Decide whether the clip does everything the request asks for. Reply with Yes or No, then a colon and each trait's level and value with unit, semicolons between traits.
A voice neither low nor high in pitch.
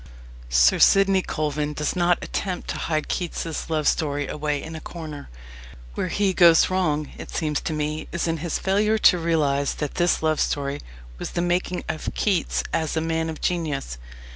Yes: medium, 160 Hz